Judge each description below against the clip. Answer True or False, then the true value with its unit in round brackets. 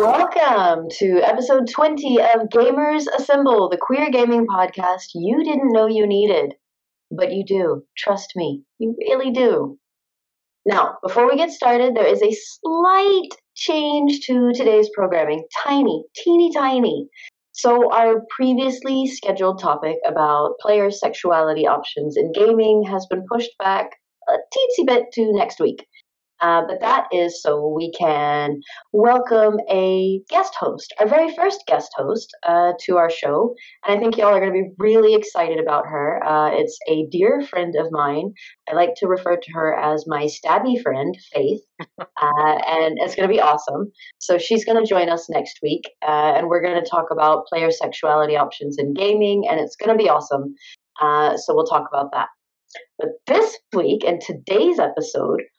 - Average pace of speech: True (170 wpm)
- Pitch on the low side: False (205 Hz)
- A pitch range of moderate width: False (7.8 semitones)